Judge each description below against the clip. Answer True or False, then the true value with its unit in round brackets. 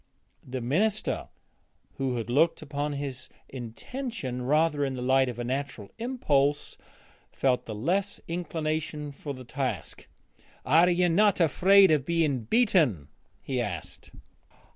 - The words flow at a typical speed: False (125 wpm)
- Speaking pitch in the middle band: True (145 Hz)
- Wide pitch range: False (4.8 semitones)